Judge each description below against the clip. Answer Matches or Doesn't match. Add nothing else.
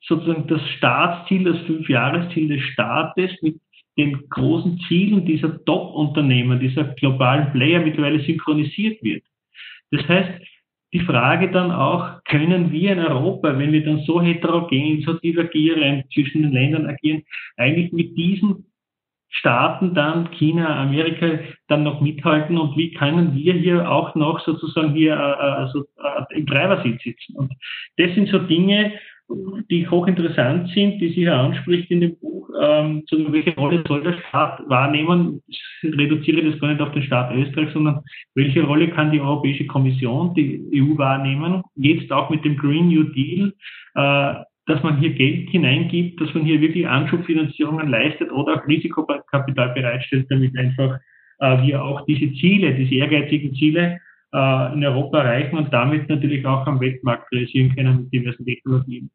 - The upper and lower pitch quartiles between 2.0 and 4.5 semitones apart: Matches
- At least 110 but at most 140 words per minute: Doesn't match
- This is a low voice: Doesn't match